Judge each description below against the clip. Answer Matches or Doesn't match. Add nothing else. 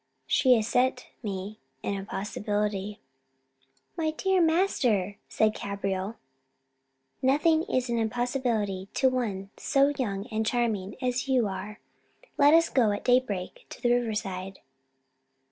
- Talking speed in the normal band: Doesn't match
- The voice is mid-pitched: Doesn't match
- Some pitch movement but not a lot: Matches